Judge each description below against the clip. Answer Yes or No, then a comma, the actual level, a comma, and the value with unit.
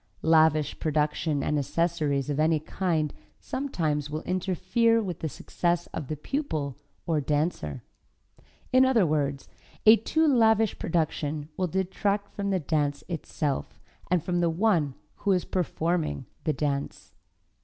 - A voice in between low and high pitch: Yes, medium, 160 Hz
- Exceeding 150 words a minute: No, slow, 135 wpm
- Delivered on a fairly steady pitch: No, average, 4.2 semitones